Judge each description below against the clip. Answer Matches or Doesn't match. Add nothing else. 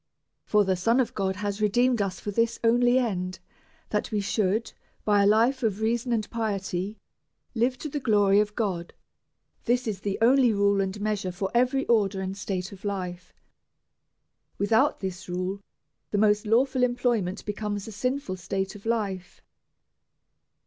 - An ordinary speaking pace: Matches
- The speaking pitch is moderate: Doesn't match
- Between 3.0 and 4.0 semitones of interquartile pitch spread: Matches